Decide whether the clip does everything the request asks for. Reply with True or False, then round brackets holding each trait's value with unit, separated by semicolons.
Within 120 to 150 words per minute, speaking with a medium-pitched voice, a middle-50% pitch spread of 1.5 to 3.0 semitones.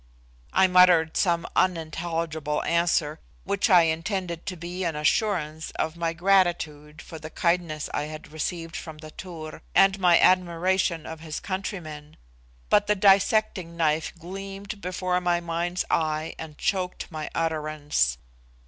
True (140 wpm; 170 Hz; 2.7 semitones)